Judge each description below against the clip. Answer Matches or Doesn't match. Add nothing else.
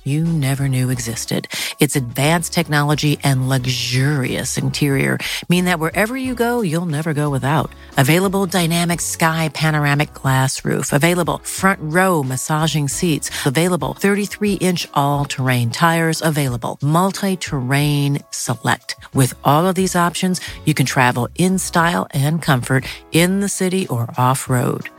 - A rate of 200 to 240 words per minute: Doesn't match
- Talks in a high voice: Doesn't match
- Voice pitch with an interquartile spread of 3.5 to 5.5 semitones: Matches